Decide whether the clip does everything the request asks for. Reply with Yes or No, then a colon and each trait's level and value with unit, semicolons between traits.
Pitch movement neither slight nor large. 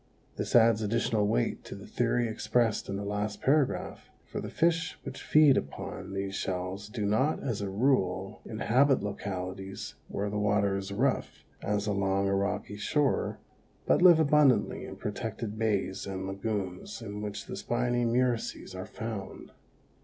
Yes: average, 3.4 semitones